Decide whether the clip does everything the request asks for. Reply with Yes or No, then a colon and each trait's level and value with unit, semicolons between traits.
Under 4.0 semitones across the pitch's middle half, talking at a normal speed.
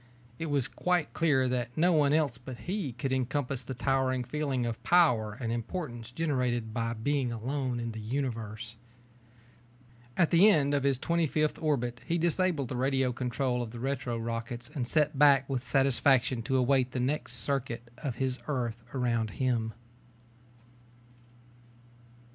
Yes: average, 3.2 semitones; average, 155 wpm